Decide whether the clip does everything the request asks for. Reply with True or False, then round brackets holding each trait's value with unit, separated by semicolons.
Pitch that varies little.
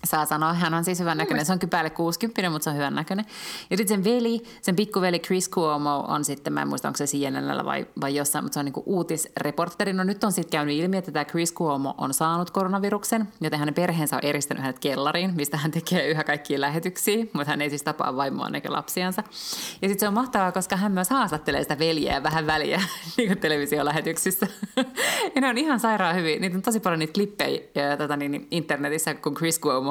False (4.6 semitones)